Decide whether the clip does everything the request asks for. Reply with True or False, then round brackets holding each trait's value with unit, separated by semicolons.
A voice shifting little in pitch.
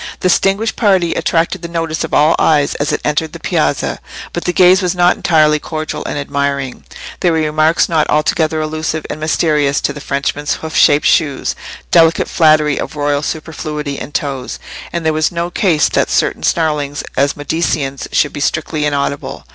True (2.2 semitones)